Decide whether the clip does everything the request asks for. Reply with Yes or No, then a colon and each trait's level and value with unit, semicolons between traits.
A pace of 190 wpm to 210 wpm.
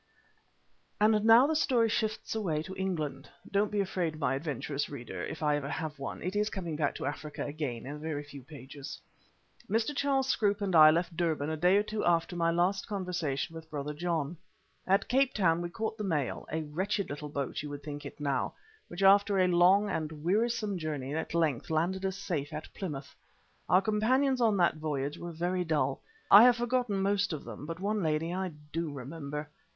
Yes: average, 200 wpm